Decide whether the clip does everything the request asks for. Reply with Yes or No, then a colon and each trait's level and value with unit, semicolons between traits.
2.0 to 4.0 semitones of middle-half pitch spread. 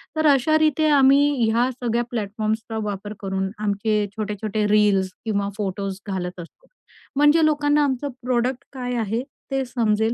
No: average, 4.8 semitones